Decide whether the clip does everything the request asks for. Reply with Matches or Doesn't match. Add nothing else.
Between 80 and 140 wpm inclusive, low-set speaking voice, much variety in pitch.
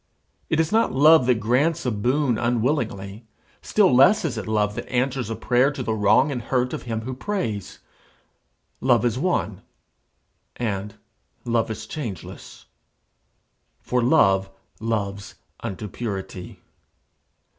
Doesn't match